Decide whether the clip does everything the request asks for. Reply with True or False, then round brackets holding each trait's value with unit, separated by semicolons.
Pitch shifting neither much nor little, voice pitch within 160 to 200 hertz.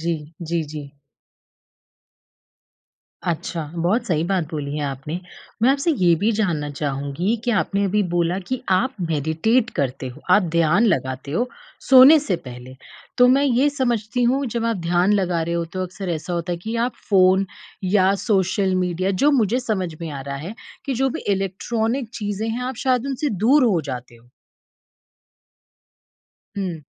False (6.2 semitones; 190 Hz)